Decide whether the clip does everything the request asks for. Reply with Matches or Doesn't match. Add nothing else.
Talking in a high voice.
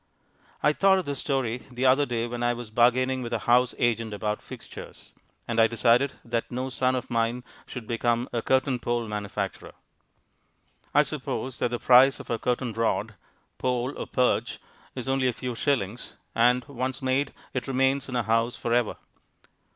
Doesn't match